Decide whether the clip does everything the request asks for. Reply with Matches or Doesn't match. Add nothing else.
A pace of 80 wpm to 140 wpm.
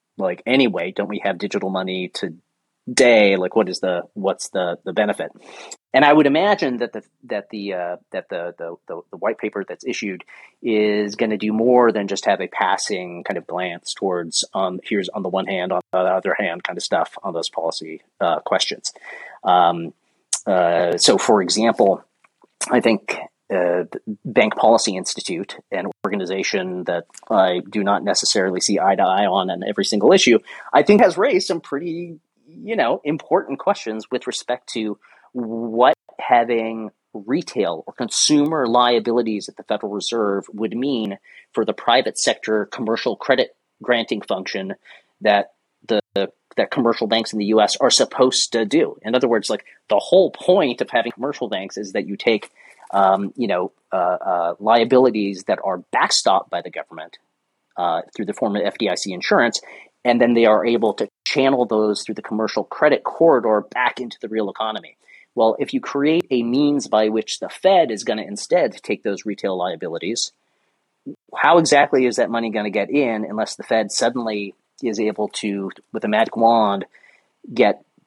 Doesn't match